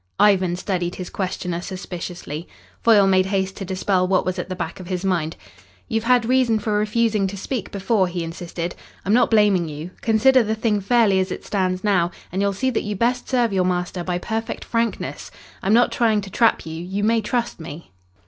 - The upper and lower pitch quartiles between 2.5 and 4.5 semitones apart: Yes, average, 3.6 semitones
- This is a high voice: Yes, high, 195 Hz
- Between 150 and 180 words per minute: No, fast, 205 wpm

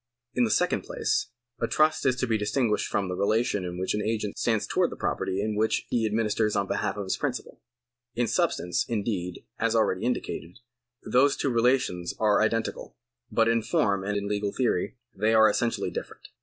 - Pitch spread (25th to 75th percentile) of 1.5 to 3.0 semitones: Yes, narrow, 2.5 semitones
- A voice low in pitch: Yes, low, 110 Hz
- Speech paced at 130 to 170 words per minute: No, average, 185 wpm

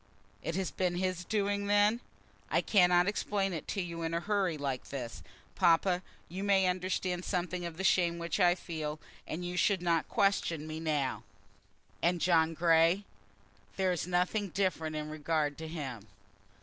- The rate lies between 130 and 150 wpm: No, average, 165 wpm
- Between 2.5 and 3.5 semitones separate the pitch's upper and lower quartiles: Yes, average, 2.8 semitones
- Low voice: No, medium, 175 Hz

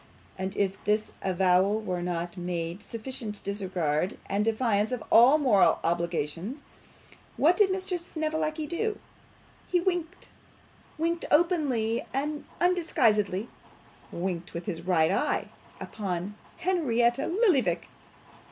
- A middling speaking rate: No, slow, 115 wpm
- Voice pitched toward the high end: Yes, high, 220 Hz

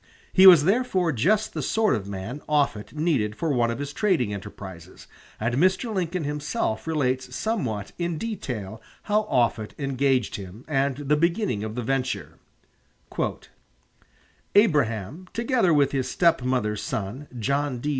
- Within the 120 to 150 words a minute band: Yes, average, 140 wpm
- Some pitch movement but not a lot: No, wide, 7.5 semitones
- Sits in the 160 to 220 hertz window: No, medium, 140 Hz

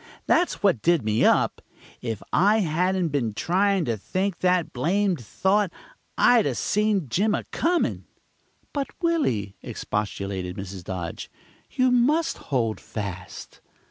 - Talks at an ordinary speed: No, slow, 130 wpm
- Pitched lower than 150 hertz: No, medium, 175 Hz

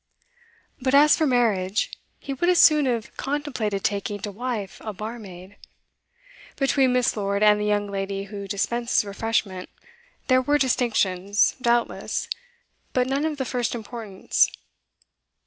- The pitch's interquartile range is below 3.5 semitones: No, average, 4.3 semitones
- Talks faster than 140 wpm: No, slow, 135 wpm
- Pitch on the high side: Yes, high, 225 Hz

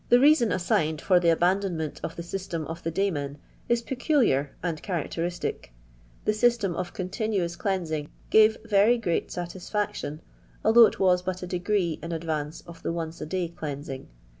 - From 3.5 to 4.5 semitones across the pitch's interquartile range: Yes, average, 3.9 semitones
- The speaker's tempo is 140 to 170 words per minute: Yes, average, 160 wpm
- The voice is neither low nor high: Yes, medium, 175 Hz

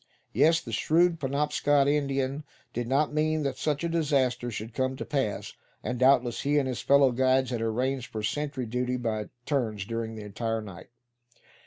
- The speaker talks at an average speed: Yes, average, 175 wpm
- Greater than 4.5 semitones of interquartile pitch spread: No, average, 3.7 semitones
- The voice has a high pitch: No, low, 130 Hz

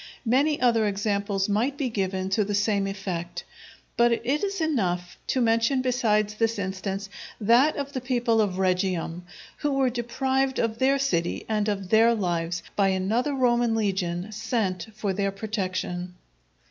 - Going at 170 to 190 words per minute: No, average, 155 wpm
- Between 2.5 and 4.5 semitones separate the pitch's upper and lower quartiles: Yes, average, 4.2 semitones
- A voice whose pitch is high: Yes, high, 215 Hz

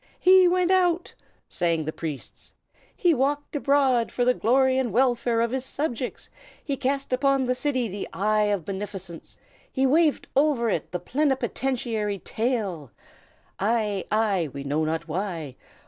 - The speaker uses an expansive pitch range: Yes, wide, 5.8 semitones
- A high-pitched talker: Yes, high, 240 Hz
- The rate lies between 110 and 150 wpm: Yes, average, 145 wpm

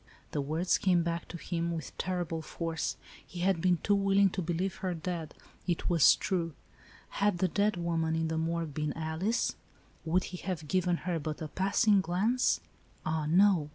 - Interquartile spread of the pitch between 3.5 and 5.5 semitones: No, narrow, 2.5 semitones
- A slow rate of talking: No, average, 185 wpm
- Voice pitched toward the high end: No, medium, 170 Hz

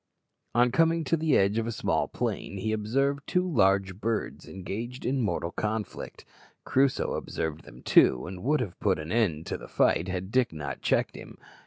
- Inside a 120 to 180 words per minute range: No, average, 190 wpm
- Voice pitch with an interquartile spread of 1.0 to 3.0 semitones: No, wide, 5.5 semitones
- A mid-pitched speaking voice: No, low, 110 Hz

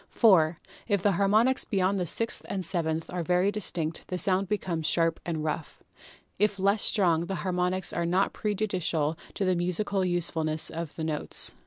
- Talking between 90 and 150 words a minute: No, average, 170 wpm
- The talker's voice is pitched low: No, medium, 180 Hz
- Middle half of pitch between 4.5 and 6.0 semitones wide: No, average, 3.2 semitones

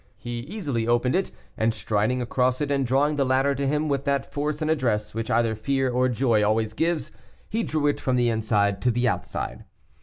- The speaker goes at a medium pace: No, fast, 210 wpm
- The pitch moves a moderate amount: Yes, average, 3.8 semitones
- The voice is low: Yes, low, 125 Hz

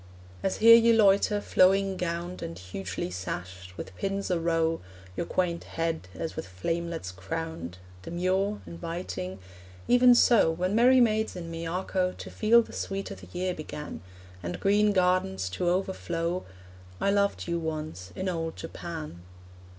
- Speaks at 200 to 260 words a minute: No, average, 150 wpm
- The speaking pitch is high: No, medium, 170 Hz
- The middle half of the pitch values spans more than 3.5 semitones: Yes, average, 3.9 semitones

